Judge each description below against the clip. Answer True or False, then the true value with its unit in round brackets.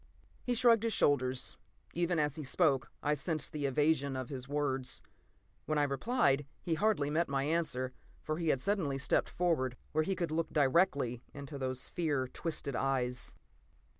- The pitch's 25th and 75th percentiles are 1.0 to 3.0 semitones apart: False (3.8 semitones)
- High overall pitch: False (145 Hz)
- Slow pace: False (170 wpm)